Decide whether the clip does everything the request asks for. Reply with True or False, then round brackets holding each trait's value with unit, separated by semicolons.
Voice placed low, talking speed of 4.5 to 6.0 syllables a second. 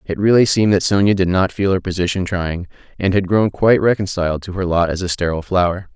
False (95 Hz; 6.4 syllables/s)